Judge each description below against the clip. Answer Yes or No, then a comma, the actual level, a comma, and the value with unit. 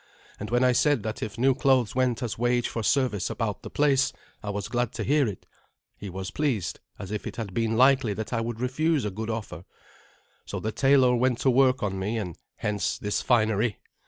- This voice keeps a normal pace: No, fast, 215 wpm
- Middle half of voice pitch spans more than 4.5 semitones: No, average, 3.6 semitones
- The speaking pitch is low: Yes, low, 115 Hz